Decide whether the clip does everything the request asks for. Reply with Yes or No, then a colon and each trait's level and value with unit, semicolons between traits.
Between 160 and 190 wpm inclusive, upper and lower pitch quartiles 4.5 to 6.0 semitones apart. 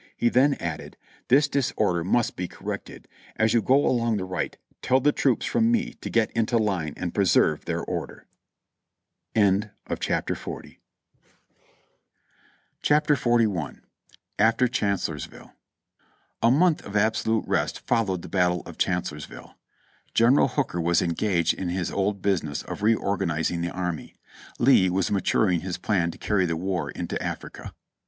No: average, 140 wpm; average, 5.1 semitones